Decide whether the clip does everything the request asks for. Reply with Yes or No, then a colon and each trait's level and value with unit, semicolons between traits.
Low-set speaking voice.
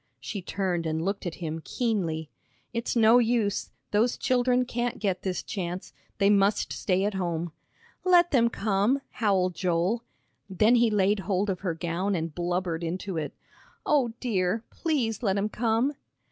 No: high, 200 Hz